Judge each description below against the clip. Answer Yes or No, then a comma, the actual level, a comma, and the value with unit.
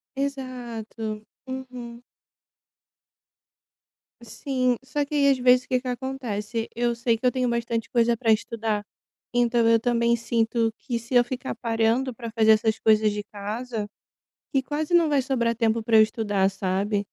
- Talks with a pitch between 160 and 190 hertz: No, high, 235 Hz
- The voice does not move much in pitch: Yes, narrow, 2.3 semitones